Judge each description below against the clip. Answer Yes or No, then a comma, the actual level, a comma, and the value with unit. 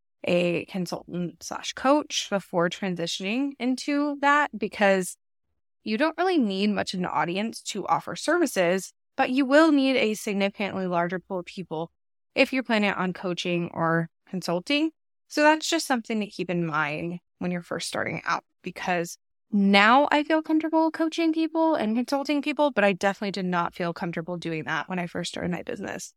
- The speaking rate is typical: Yes, average, 170 wpm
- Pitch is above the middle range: Yes, high, 200 Hz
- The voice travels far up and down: Yes, wide, 8.1 semitones